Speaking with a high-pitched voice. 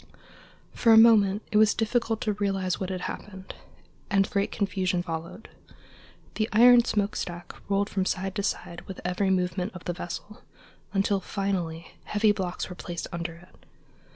Yes: high, 195 Hz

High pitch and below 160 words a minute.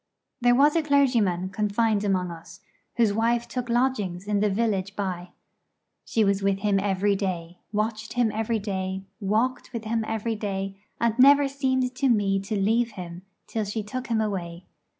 No: high, 210 Hz; average, 170 wpm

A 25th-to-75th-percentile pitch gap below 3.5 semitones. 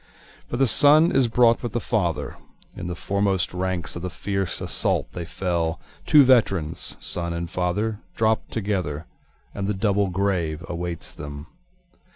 No: average, 4.3 semitones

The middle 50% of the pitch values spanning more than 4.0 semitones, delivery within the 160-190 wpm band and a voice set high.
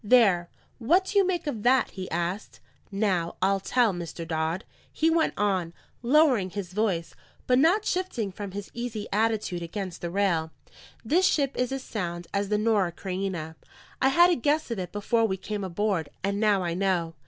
Yes: wide, 5.4 semitones; average, 185 wpm; high, 205 Hz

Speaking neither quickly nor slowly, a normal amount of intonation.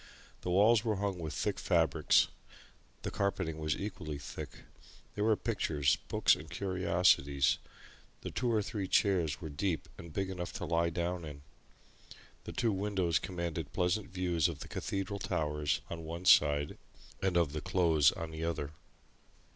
Yes: average, 160 wpm; average, 3.7 semitones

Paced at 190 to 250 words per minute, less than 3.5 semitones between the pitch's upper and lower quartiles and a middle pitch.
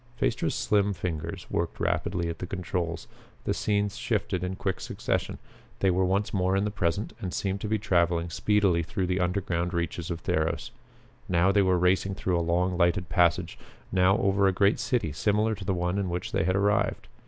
No: average, 195 wpm; narrow, 2.4 semitones; very low, 90 Hz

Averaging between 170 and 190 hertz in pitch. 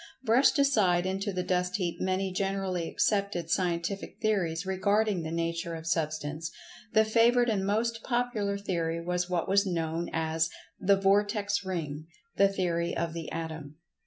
Yes: medium, 185 Hz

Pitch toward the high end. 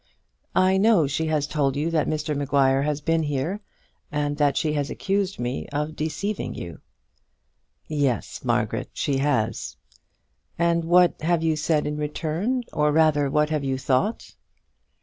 No: medium, 150 Hz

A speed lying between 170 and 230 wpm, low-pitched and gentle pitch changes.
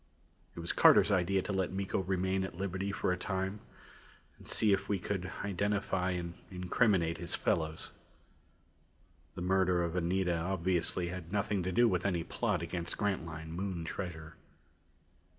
No: average, 150 wpm; very low, 95 Hz; narrow, 2.1 semitones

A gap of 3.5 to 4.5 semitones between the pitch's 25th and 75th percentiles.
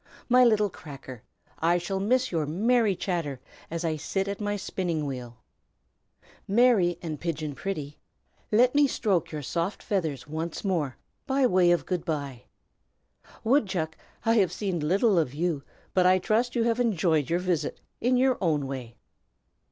No: wide, 5.4 semitones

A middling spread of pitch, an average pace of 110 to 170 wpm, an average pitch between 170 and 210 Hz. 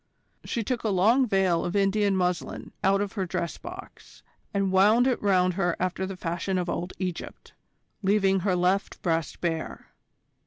No: narrow, 2.1 semitones; average, 165 wpm; high, 190 Hz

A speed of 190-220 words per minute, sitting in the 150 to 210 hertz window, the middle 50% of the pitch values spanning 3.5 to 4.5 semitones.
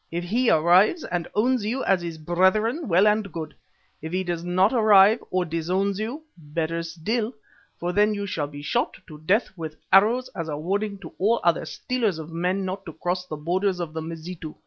Yes: average, 200 wpm; medium, 185 Hz; average, 4.1 semitones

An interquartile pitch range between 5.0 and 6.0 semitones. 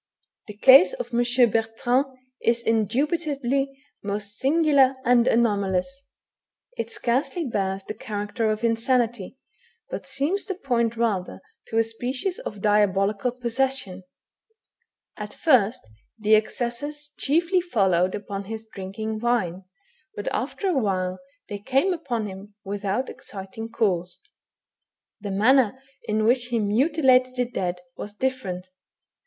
No: average, 4.4 semitones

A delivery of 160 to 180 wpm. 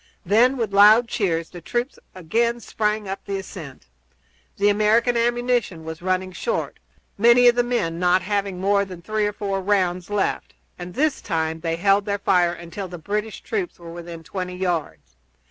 Yes: average, 175 wpm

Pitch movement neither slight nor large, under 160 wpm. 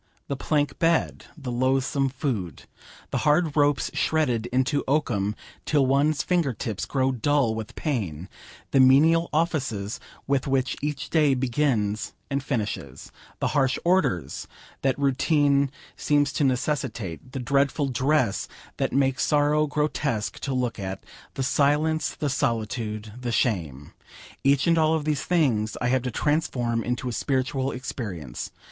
Yes: average, 3.9 semitones; average, 140 wpm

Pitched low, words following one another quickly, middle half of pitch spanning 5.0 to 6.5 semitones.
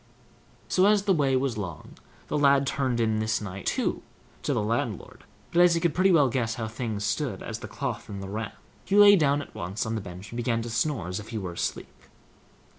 Yes: low, 115 Hz; fast, 240 wpm; wide, 5.6 semitones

